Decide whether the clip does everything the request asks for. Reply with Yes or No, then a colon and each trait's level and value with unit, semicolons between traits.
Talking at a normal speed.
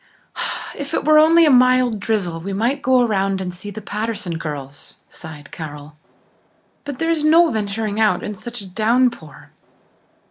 Yes: average, 165 wpm